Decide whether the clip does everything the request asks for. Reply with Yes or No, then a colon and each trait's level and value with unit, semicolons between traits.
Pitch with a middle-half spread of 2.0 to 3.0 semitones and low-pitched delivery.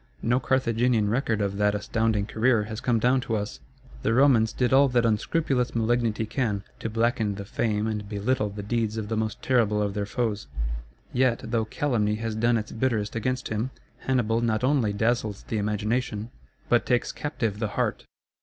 Yes: narrow, 2.5 semitones; low, 115 Hz